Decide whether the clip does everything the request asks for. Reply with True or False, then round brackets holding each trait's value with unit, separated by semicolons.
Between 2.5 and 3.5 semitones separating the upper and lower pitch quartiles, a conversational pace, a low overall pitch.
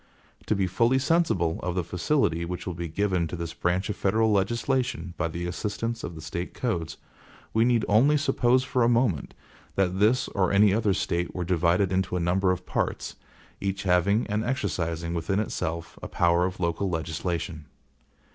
False (4.6 semitones; 180 wpm; 95 Hz)